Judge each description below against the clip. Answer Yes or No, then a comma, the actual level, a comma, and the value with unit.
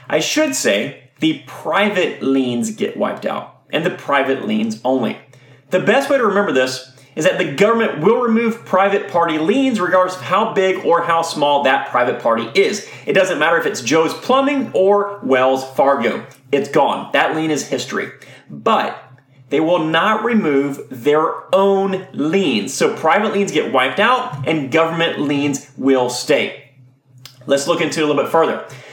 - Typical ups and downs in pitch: No, wide, 6.8 semitones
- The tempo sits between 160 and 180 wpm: Yes, average, 170 wpm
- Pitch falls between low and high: Yes, medium, 160 Hz